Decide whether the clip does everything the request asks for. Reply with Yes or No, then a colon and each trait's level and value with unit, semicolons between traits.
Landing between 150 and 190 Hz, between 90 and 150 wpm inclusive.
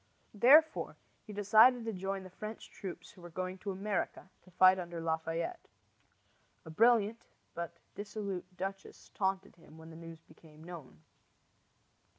Yes: medium, 185 Hz; average, 145 wpm